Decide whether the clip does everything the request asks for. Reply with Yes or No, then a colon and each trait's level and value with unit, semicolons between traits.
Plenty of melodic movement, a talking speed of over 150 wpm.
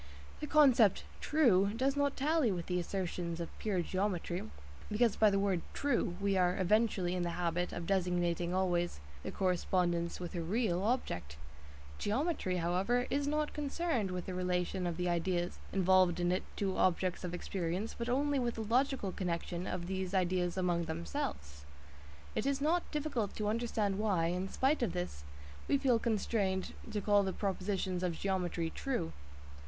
No: average, 4.6 semitones; average, 165 wpm